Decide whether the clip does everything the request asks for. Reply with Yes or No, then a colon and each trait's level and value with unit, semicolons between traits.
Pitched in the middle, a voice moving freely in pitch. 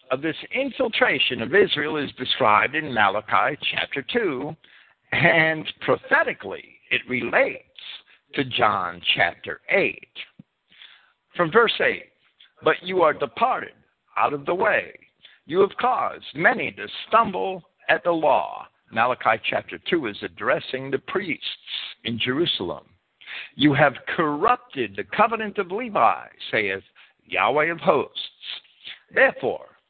Yes: medium, 170 Hz; wide, 7.9 semitones